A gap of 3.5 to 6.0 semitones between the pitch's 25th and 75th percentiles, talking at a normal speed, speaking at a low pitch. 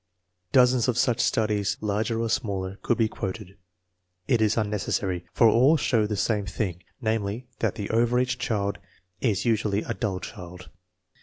No: average, 2.8 semitones; average, 160 wpm; low, 110 Hz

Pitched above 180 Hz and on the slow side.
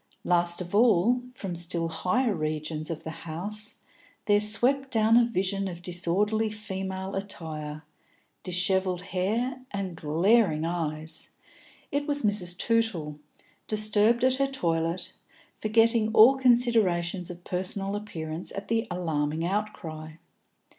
Yes: high, 190 Hz; slow, 120 wpm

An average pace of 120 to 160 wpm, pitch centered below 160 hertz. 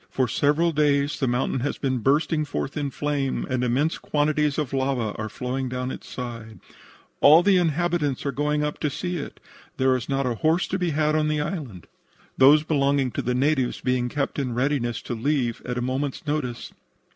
No: average, 195 wpm; medium, 140 Hz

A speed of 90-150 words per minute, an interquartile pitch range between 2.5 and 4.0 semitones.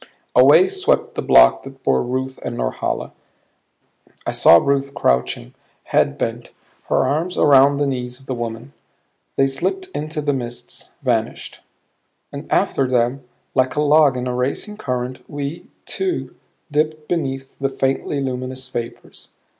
Yes: average, 145 wpm; average, 2.8 semitones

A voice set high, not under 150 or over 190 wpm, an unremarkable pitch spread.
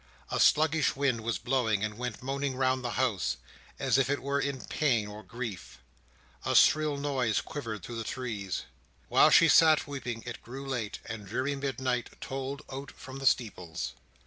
No: low, 130 Hz; average, 175 wpm; average, 3.7 semitones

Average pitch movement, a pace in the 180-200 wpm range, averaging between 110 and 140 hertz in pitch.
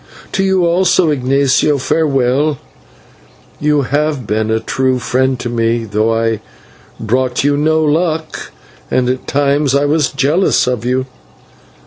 No: average, 3.4 semitones; average, 140 wpm; low, 135 Hz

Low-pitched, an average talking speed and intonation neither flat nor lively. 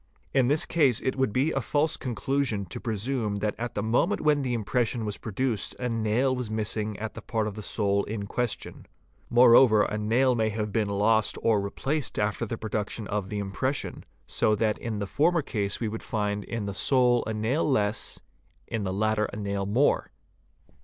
Yes: low, 110 Hz; average, 195 wpm; average, 3.3 semitones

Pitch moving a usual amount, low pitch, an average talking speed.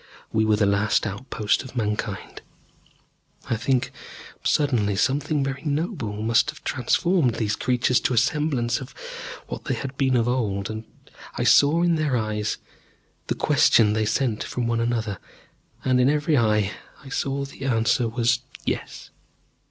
Yes: average, 4.0 semitones; low, 120 Hz; average, 160 wpm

